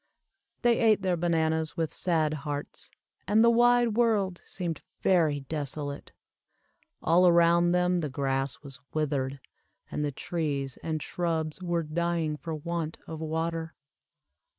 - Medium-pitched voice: Yes, medium, 165 Hz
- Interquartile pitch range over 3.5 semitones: No, average, 2.8 semitones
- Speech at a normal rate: No, slow, 130 wpm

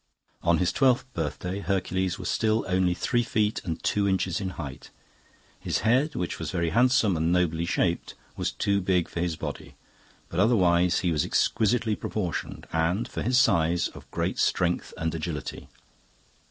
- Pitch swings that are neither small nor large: Yes, average, 3.7 semitones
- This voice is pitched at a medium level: No, very low, 90 Hz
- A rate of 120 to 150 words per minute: No, average, 165 wpm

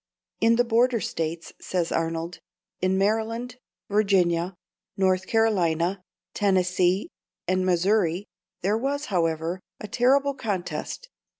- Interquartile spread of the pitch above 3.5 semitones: Yes, average, 4.2 semitones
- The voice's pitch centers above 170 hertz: Yes, high, 190 Hz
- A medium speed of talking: No, slow, 105 wpm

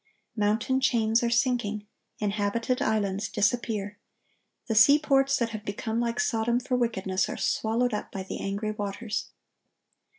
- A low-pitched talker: No, high, 220 Hz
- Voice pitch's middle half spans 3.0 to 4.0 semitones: No, narrow, 2.6 semitones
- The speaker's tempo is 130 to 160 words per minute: Yes, slow, 135 wpm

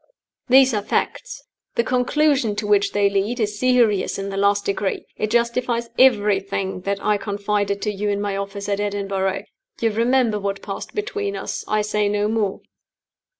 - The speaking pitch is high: Yes, high, 210 Hz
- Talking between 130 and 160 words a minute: No, average, 170 wpm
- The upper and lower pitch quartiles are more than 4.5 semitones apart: No, average, 2.8 semitones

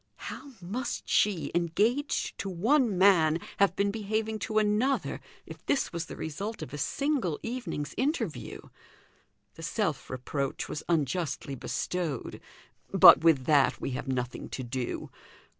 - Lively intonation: Yes, wide, 6.8 semitones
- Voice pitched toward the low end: No, medium, 180 Hz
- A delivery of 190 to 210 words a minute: No, average, 140 wpm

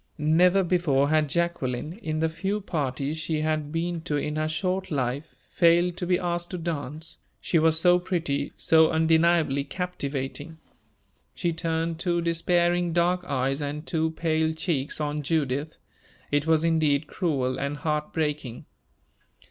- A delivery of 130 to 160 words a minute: Yes, average, 150 wpm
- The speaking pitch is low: No, medium, 160 Hz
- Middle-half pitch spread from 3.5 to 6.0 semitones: No, average, 2.7 semitones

